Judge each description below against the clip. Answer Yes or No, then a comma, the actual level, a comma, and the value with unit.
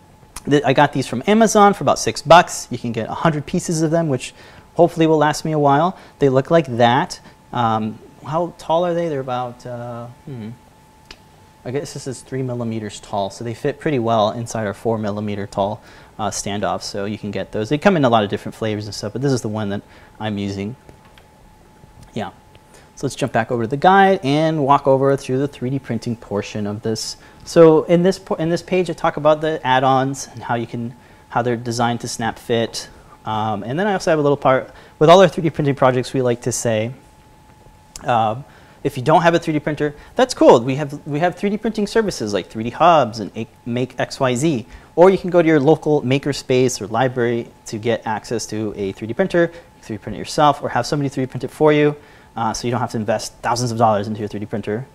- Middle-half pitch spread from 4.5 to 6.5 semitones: Yes, wide, 5.4 semitones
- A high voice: No, low, 130 Hz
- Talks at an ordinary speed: No, fast, 225 wpm